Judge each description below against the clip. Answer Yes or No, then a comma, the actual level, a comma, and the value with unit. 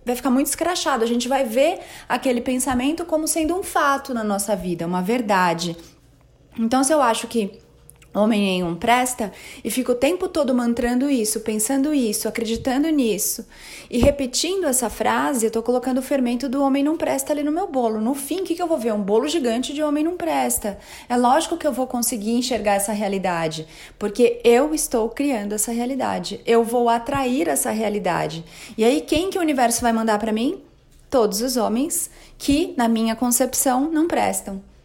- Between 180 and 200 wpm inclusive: Yes, fast, 185 wpm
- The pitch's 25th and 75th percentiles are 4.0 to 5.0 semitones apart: Yes, average, 4.3 semitones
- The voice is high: Yes, high, 245 Hz